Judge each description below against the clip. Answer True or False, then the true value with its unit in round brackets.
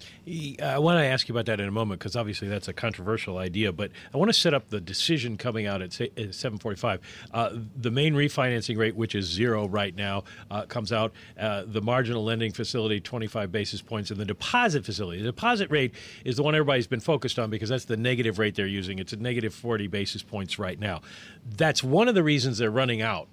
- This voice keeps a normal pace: False (220 wpm)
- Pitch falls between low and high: False (110 Hz)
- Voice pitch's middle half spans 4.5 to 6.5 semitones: False (3.3 semitones)